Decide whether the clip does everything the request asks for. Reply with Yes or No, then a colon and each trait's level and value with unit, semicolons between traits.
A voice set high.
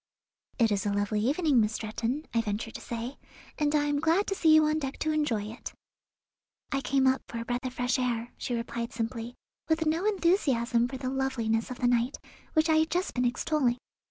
Yes: very high, 255 Hz